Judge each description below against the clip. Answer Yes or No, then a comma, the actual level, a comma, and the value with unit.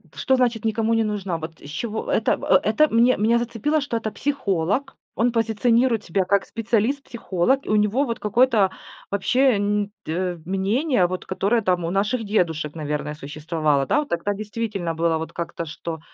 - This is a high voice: Yes, high, 210 Hz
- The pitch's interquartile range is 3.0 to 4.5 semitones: No, average, 5.3 semitones